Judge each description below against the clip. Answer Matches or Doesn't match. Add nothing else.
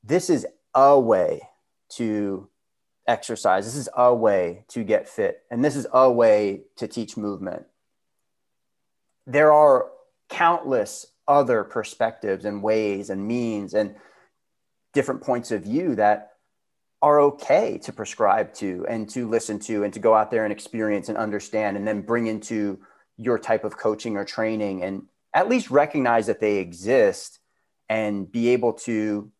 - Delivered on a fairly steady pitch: Doesn't match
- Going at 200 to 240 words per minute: Doesn't match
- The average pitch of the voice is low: Matches